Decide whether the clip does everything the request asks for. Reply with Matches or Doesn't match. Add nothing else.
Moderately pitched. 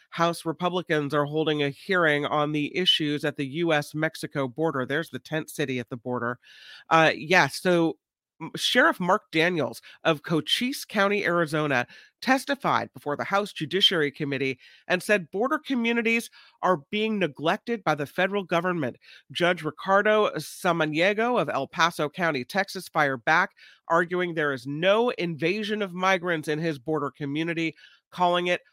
Matches